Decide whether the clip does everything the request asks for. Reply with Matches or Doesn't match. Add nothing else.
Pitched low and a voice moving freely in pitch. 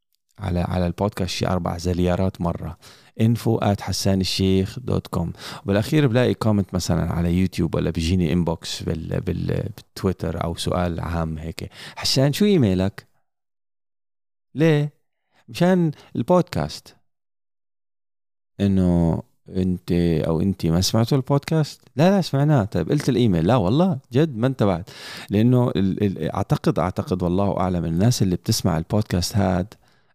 Matches